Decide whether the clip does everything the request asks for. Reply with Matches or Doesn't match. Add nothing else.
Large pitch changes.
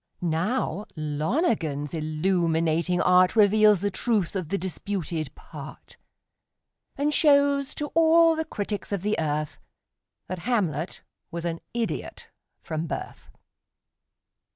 Matches